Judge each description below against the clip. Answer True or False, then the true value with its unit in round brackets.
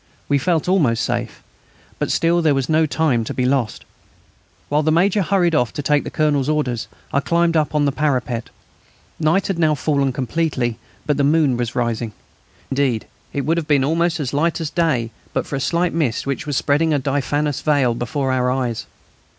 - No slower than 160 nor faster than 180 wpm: False (195 wpm)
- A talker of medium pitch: True (145 Hz)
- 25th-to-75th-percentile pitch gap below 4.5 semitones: True (3.8 semitones)